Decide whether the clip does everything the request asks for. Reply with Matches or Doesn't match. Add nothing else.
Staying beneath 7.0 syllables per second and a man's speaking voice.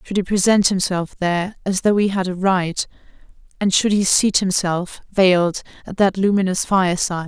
Doesn't match